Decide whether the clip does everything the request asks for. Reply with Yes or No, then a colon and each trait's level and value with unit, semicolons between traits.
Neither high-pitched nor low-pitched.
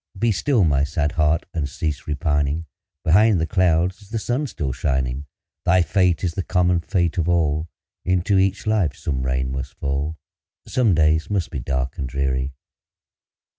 No: very low, 80 Hz